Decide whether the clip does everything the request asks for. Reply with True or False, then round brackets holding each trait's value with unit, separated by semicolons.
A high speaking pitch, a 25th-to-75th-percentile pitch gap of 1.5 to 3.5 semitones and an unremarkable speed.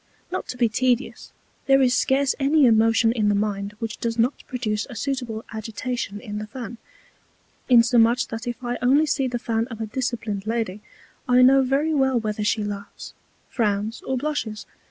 True (235 Hz; 3.0 semitones; 175 wpm)